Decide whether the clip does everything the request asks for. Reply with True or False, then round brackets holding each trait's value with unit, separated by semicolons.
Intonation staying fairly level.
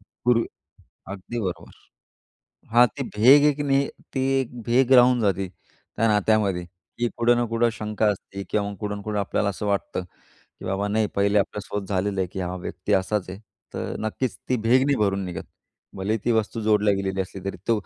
False (3.2 semitones)